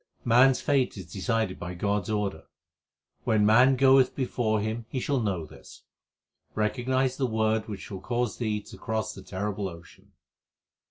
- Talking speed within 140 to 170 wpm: Yes, average, 165 wpm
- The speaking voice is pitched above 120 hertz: No, low, 110 Hz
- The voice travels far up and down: No, average, 3.6 semitones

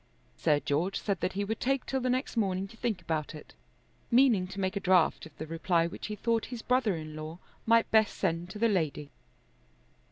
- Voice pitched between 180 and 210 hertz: Yes, high, 190 Hz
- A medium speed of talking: No, fast, 215 wpm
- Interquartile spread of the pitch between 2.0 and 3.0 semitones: No, wide, 5.5 semitones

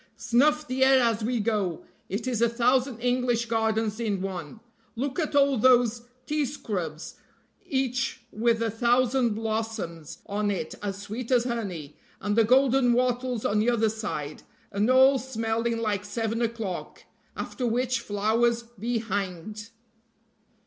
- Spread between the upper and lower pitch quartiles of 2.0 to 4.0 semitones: Yes, average, 2.9 semitones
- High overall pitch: Yes, high, 230 Hz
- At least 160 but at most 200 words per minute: No, average, 145 wpm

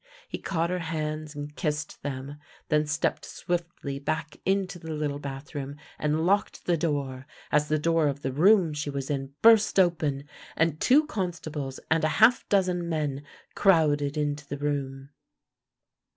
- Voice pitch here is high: No, medium, 150 Hz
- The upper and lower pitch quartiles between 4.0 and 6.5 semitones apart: No, average, 3.0 semitones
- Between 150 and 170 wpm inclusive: Yes, average, 155 wpm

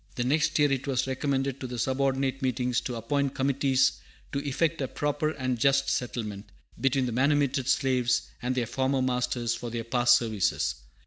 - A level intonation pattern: Yes, narrow, 2.1 semitones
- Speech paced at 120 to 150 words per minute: No, average, 175 wpm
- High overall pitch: No, low, 130 Hz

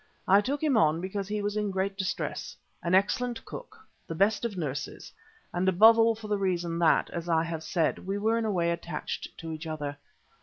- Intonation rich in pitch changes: No, average, 4.1 semitones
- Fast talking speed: Yes, fast, 215 wpm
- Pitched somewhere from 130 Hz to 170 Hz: No, high, 190 Hz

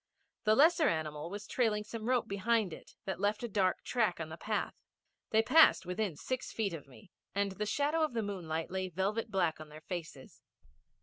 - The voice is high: Yes, high, 200 Hz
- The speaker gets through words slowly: No, average, 195 wpm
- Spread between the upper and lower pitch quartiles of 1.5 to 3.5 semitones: No, average, 4.8 semitones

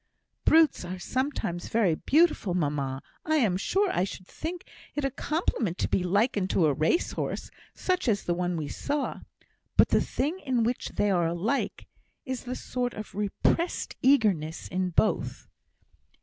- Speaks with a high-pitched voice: Yes, high, 215 Hz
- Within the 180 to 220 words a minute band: No, average, 165 wpm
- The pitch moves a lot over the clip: Yes, wide, 7.9 semitones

